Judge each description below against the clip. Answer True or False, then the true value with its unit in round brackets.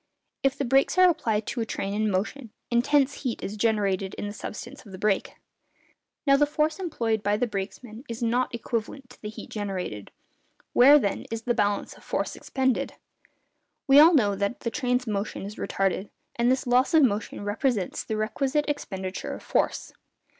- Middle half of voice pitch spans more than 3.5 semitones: True (4.6 semitones)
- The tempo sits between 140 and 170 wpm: False (180 wpm)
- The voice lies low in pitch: False (230 Hz)